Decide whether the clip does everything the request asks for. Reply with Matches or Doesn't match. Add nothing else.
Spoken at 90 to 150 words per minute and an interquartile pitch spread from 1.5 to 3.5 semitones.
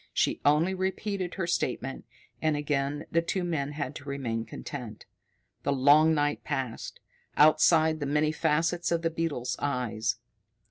Matches